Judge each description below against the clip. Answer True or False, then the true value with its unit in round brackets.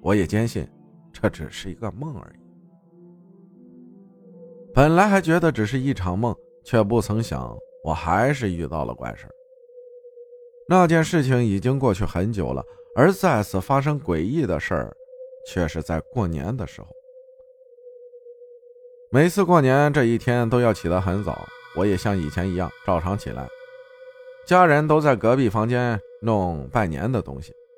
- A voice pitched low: False (150 Hz)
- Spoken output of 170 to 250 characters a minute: True (220 characters per minute)